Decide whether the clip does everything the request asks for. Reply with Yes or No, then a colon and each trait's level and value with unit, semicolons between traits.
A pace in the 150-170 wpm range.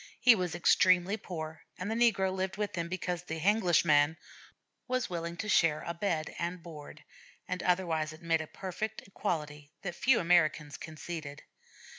Yes: average, 155 wpm